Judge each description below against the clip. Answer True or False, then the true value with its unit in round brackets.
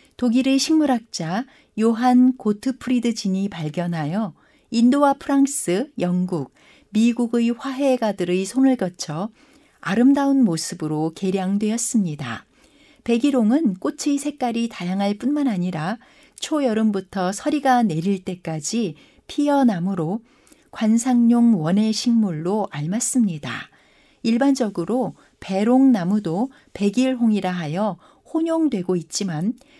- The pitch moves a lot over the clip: True (5.7 semitones)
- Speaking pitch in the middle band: False (230 Hz)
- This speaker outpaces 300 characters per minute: False (255 characters per minute)